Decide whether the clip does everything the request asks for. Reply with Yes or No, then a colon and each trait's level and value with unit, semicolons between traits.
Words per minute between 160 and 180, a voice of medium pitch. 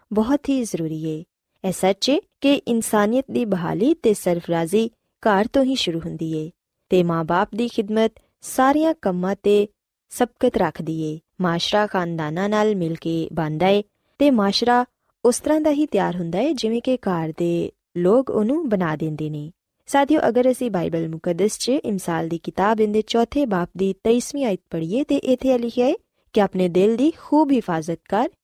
No: fast, 165 wpm; high, 205 Hz